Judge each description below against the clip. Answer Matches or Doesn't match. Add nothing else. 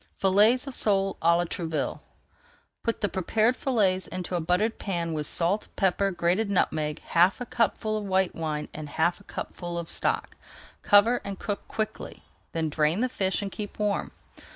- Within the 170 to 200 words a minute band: Matches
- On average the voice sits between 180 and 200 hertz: Matches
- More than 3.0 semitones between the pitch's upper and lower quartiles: Matches